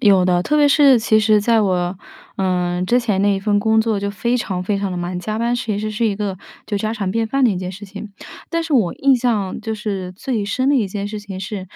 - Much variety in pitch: No, average, 3.2 semitones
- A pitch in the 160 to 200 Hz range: No, high, 210 Hz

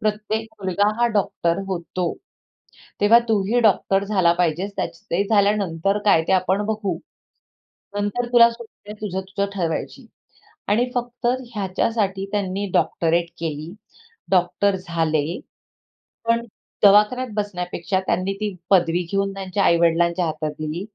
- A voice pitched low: No, high, 195 Hz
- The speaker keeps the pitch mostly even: No, average, 3.4 semitones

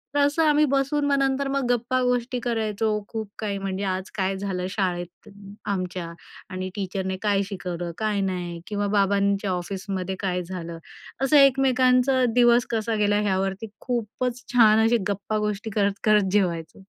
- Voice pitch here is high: Yes, high, 205 Hz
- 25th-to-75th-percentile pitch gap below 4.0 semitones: No, average, 4.3 semitones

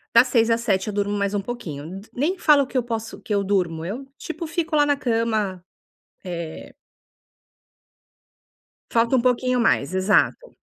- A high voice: Yes, high, 225 Hz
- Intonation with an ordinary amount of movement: Yes, average, 4.7 semitones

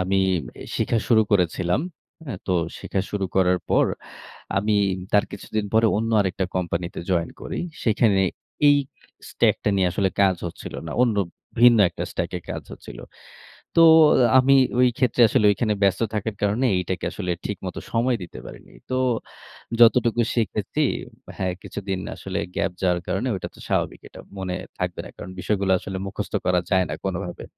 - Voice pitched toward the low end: Yes, low, 100 Hz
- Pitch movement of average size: Yes, average, 3.5 semitones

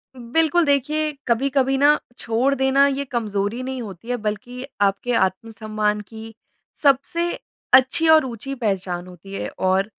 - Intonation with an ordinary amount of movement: Yes, average, 4.8 semitones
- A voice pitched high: Yes, high, 245 Hz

